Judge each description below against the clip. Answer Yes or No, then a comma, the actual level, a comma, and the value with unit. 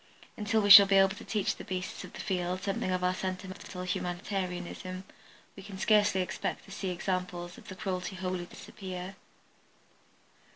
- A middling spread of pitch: No, narrow, 1.3 semitones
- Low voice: No, medium, 185 Hz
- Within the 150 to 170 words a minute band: Yes, average, 160 wpm